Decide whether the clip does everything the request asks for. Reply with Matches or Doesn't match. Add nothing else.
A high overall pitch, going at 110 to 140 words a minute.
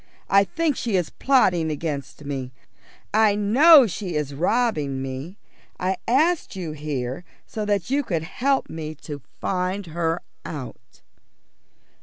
Doesn't match